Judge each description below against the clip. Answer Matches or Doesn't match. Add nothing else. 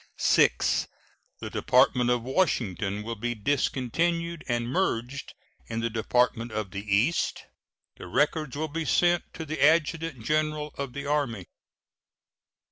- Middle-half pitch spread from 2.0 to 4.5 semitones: Doesn't match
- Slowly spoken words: Matches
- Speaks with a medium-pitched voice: Doesn't match